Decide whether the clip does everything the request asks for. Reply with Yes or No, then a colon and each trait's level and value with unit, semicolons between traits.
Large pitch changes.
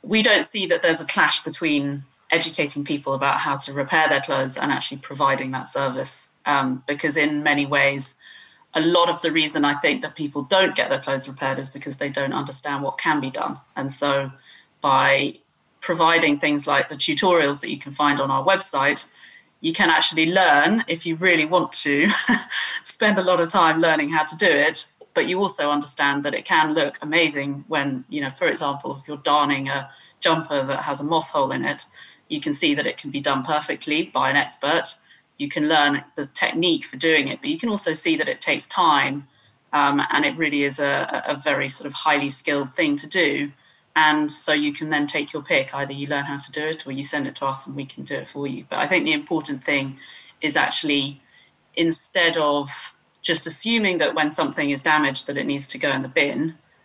No: average, 2.8 semitones